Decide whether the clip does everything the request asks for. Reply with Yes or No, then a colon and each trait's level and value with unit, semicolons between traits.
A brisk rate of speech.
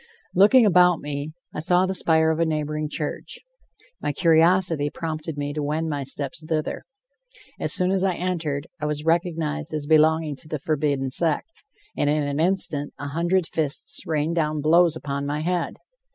No: average, 175 wpm